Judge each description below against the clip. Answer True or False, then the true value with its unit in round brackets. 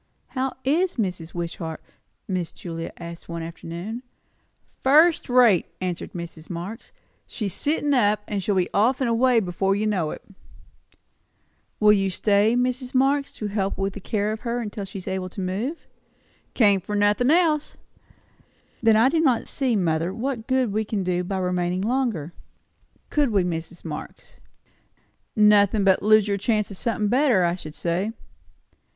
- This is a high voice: True (205 Hz)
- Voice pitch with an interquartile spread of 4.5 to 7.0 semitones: True (5.2 semitones)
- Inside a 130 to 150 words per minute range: False (160 wpm)